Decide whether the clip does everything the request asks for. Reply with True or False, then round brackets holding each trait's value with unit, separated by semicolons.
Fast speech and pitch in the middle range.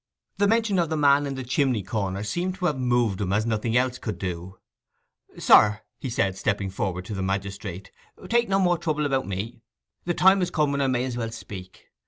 False (215 wpm; 120 Hz)